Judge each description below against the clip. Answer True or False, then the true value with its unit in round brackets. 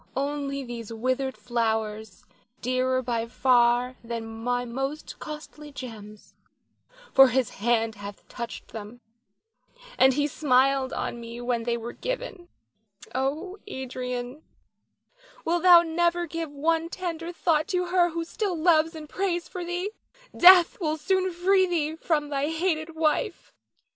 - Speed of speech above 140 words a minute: False (135 wpm)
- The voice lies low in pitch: False (285 Hz)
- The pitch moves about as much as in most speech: False (5.7 semitones)